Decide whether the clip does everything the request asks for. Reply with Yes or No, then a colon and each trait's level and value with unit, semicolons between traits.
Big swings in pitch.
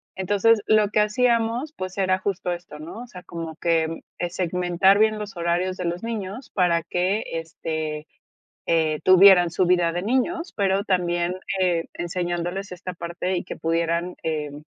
No: average, 2.9 semitones